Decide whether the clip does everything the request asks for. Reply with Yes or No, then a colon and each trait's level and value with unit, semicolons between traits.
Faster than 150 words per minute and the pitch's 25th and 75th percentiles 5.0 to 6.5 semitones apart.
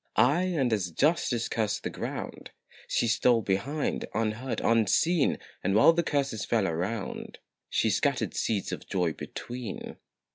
No: average, 140 wpm; wide, 5.4 semitones